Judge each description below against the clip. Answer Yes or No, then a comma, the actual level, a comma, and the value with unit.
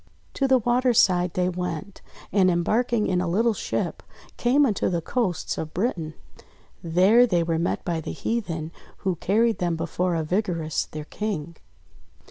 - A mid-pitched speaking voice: Yes, medium, 180 Hz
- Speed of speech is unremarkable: Yes, average, 155 wpm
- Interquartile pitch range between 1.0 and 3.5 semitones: No, average, 4.9 semitones